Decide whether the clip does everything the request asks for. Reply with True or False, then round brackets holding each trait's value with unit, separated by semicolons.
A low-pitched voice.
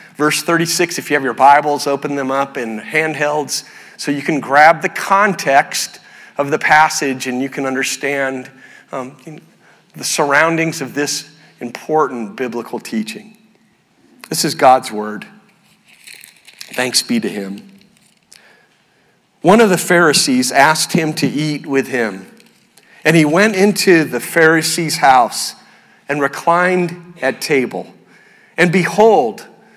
False (155 Hz)